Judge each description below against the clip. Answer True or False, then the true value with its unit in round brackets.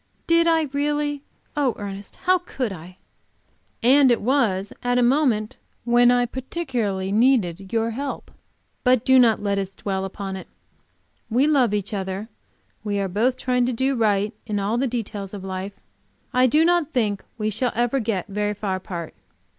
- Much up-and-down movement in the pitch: False (4.6 semitones)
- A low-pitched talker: False (230 Hz)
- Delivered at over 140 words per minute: True (170 wpm)